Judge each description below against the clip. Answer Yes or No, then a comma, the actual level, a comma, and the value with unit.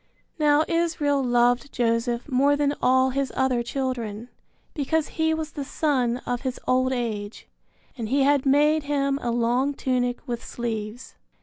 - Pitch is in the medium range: No, very high, 260 Hz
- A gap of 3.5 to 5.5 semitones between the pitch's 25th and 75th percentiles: No, average, 3.0 semitones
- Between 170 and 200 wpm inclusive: No, average, 150 wpm